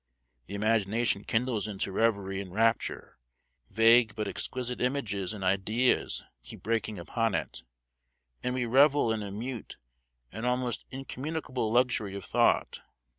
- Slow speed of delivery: Yes, slow, 130 wpm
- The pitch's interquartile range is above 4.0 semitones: No, average, 3.6 semitones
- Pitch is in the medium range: No, low, 115 Hz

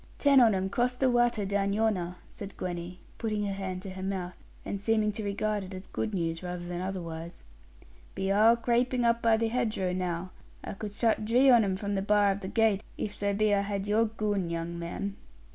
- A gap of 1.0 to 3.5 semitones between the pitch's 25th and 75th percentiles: Yes, average, 3.0 semitones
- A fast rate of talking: Yes, fast, 210 wpm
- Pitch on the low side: No, high, 200 Hz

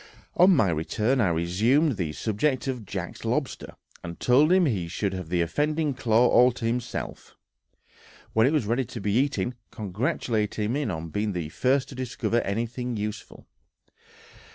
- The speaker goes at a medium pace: Yes, average, 160 wpm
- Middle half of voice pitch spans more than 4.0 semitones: Yes, average, 4.7 semitones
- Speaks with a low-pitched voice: Yes, low, 115 Hz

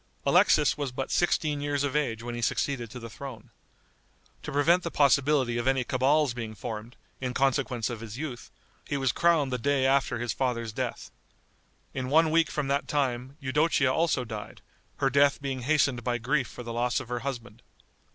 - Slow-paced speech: No, average, 190 wpm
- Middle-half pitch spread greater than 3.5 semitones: No, average, 3.1 semitones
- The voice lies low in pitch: Yes, low, 130 Hz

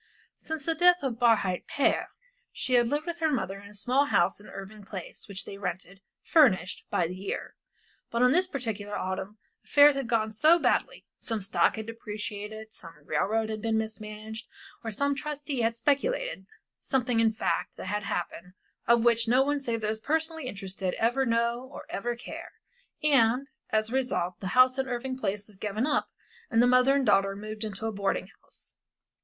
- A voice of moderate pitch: No, high, 225 Hz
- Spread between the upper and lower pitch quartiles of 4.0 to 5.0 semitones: Yes, average, 4.4 semitones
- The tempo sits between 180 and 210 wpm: Yes, average, 185 wpm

